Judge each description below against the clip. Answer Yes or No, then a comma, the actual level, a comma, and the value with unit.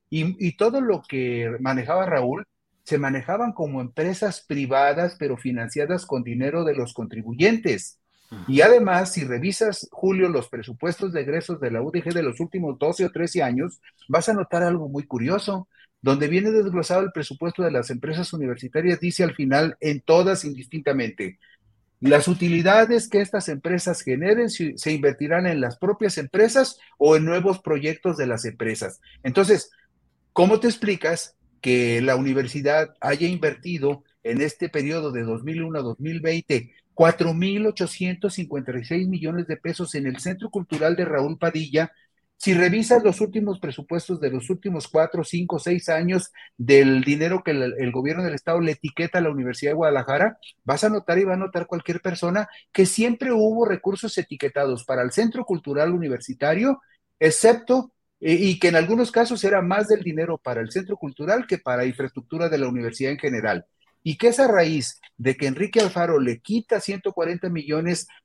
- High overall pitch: No, medium, 165 Hz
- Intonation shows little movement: No, average, 5.0 semitones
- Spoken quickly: No, average, 165 wpm